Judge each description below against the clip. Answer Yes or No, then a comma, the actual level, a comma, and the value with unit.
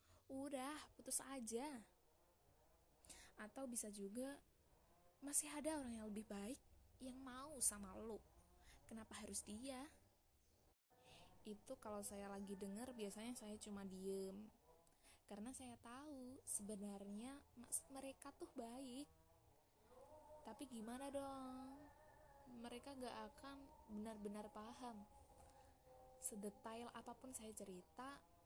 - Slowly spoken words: No, average, 100 wpm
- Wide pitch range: No, average, 4.2 semitones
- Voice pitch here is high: Yes, high, 240 Hz